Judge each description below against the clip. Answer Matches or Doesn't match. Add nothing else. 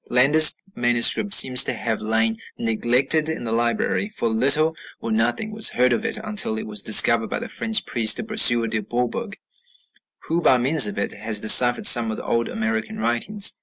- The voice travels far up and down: Matches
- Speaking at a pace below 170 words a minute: Doesn't match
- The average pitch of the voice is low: Matches